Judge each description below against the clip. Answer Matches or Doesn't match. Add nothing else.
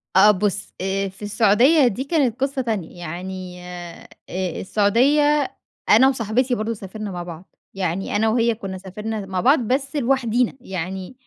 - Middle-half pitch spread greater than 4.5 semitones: Matches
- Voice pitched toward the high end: Matches